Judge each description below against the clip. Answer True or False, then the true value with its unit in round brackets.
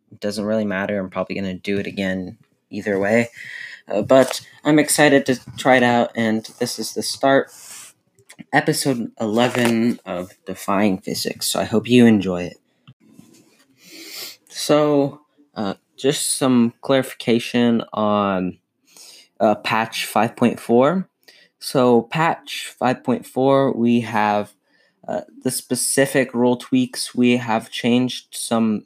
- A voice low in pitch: True (120 Hz)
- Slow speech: True (125 wpm)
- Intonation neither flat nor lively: True (3.9 semitones)